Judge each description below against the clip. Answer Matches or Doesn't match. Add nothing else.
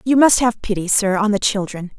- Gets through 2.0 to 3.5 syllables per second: Doesn't match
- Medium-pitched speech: Doesn't match